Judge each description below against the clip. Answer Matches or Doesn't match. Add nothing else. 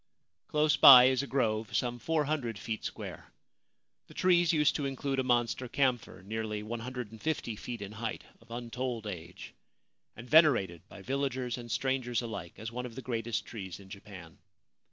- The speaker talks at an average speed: Matches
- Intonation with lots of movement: Doesn't match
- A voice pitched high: Doesn't match